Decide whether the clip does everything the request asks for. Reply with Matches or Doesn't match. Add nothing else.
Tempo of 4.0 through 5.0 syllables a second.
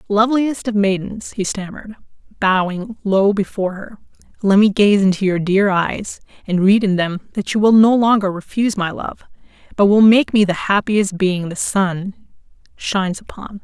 Matches